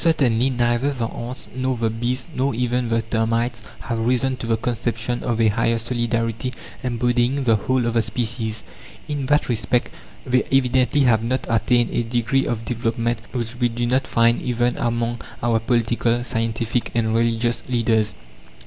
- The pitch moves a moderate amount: No, narrow, 1.5 semitones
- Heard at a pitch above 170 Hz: No, low, 120 Hz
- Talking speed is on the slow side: No, average, 165 wpm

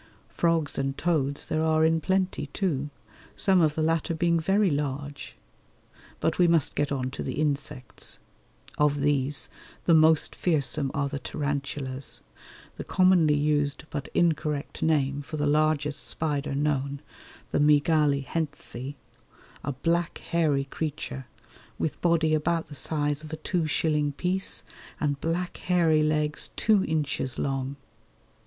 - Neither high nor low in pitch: Yes, medium, 150 Hz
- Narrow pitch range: Yes, narrow, 2.3 semitones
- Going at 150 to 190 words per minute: No, average, 140 wpm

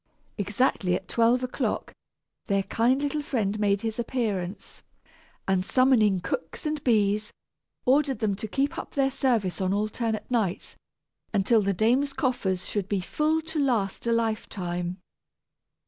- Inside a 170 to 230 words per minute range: No, average, 140 wpm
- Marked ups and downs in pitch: No, average, 4.6 semitones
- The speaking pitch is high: Yes, high, 220 Hz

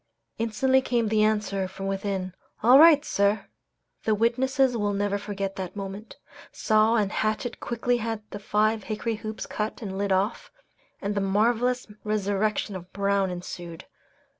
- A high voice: Yes, high, 210 Hz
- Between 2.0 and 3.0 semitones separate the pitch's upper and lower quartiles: Yes, narrow, 2.5 semitones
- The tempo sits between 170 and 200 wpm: No, average, 155 wpm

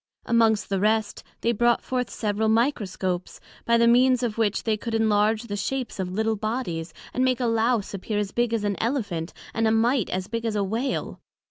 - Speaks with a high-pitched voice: Yes, high, 220 Hz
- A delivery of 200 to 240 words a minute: Yes, fast, 205 wpm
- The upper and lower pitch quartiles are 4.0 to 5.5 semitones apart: No, narrow, 2.4 semitones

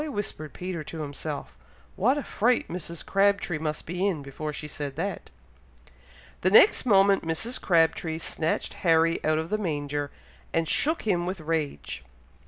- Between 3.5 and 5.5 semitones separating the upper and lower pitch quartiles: Yes, average, 4.2 semitones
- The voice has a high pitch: No, medium, 165 Hz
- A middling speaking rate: Yes, average, 155 wpm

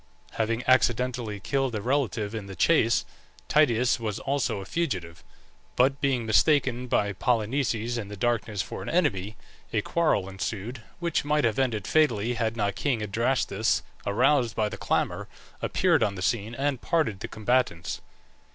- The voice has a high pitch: No, low, 115 Hz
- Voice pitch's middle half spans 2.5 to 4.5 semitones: Yes, average, 4.1 semitones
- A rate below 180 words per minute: Yes, average, 155 wpm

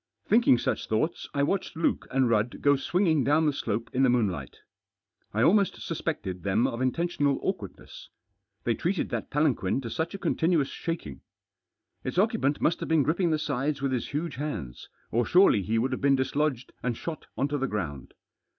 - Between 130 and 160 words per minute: No, average, 185 wpm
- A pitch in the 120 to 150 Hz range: Yes, medium, 140 Hz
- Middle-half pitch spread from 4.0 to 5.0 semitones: No, wide, 5.4 semitones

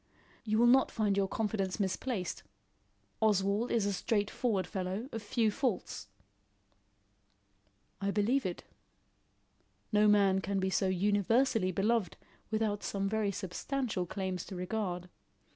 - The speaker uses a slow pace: Yes, slow, 125 wpm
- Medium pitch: No, high, 205 Hz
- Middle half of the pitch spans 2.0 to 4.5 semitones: Yes, average, 2.7 semitones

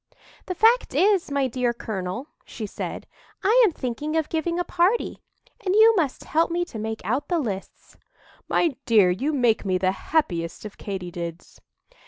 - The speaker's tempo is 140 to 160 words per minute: No, average, 175 wpm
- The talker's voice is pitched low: No, very high, 265 Hz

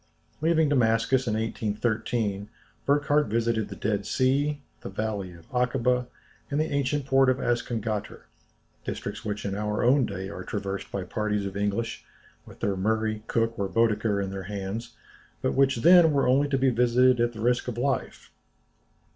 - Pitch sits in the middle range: No, low, 115 Hz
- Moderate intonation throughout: Yes, average, 3.9 semitones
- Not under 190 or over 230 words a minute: No, average, 165 wpm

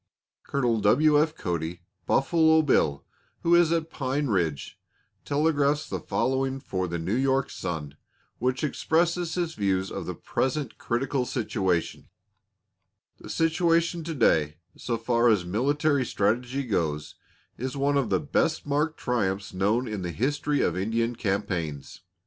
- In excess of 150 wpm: No, average, 140 wpm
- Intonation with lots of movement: Yes, wide, 7.4 semitones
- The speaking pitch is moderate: No, low, 130 Hz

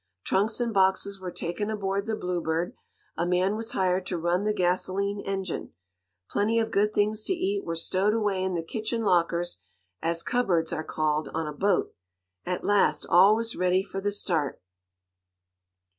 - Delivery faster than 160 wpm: Yes, average, 170 wpm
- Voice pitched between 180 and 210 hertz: Yes, high, 190 Hz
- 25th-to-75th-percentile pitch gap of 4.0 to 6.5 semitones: No, average, 3.2 semitones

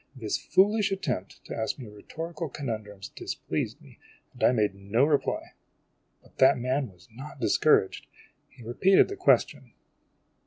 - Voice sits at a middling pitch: No, low, 130 Hz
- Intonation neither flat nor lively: No, wide, 6.5 semitones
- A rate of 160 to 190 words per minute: No, average, 145 wpm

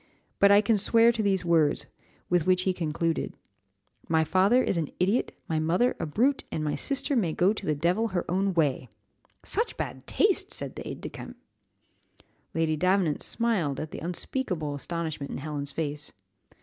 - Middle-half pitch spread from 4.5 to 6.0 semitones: Yes, average, 5.0 semitones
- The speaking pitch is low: No, medium, 175 Hz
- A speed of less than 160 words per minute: No, average, 175 wpm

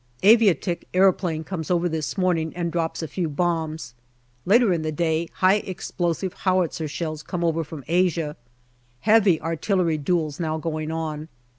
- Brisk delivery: No, average, 150 wpm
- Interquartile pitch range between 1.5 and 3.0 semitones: Yes, narrow, 2.6 semitones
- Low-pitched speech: No, medium, 165 Hz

